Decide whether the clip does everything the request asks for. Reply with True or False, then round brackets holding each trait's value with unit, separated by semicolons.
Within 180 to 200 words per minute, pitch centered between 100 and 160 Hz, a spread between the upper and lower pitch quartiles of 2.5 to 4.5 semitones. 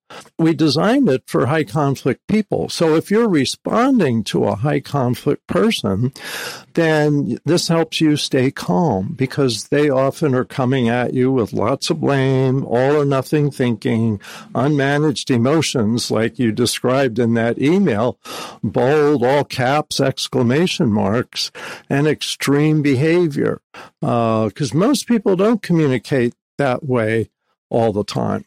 False (135 wpm; 140 Hz; 4.1 semitones)